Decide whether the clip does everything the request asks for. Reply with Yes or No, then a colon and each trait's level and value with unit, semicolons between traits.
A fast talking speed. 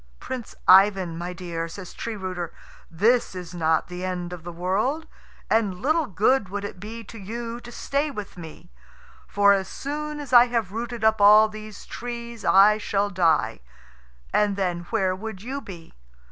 No: average, 175 wpm